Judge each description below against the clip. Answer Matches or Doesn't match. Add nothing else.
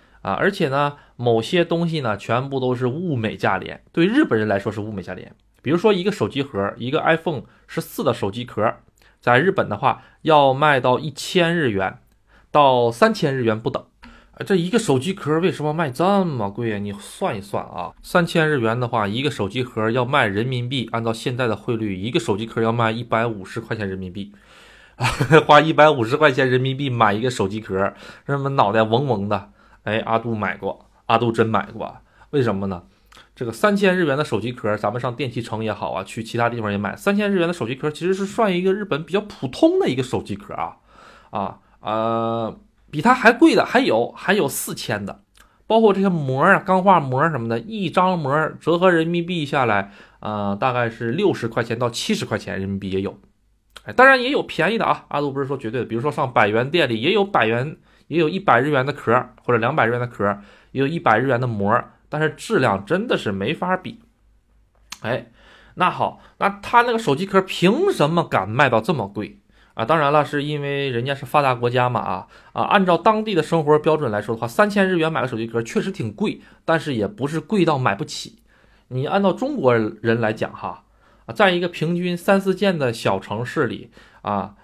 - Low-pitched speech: Matches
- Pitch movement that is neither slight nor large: Doesn't match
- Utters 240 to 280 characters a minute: Doesn't match